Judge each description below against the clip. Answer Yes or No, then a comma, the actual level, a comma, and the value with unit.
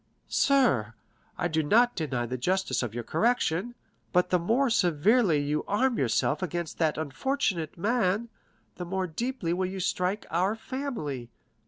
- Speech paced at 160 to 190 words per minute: No, average, 150 wpm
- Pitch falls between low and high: Yes, medium, 180 Hz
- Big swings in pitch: Yes, wide, 6.9 semitones